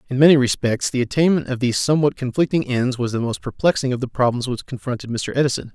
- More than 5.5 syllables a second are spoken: Yes, 6.7 syllables/s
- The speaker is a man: Yes, male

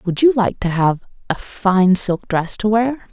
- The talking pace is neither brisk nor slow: No, fast, 210 wpm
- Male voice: No, female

